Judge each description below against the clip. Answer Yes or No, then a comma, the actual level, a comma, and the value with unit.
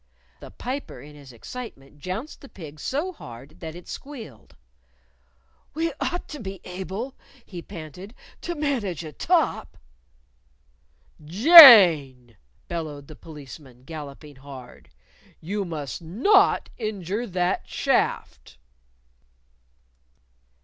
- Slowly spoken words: Yes, slow, 105 wpm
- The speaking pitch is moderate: Yes, medium, 175 Hz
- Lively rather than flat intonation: Yes, wide, 8.6 semitones